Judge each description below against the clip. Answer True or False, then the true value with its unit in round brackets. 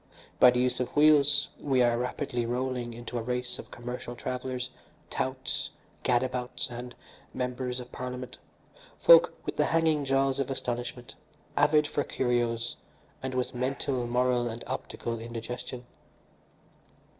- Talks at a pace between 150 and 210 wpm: False (135 wpm)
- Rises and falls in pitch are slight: True (1.4 semitones)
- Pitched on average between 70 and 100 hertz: False (125 Hz)